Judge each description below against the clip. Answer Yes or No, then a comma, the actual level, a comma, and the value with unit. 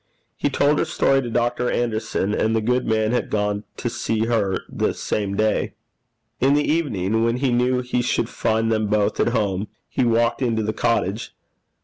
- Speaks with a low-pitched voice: Yes, low, 115 Hz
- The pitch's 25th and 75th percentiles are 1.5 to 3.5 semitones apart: Yes, narrow, 2.4 semitones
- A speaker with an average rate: Yes, average, 190 wpm